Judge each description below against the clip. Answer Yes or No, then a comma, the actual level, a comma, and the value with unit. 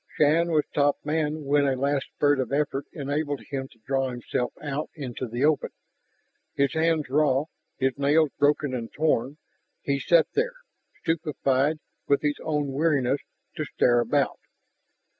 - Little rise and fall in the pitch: Yes, narrow, 2.2 semitones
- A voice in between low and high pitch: Yes, medium, 145 Hz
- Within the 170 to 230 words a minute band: No, average, 150 wpm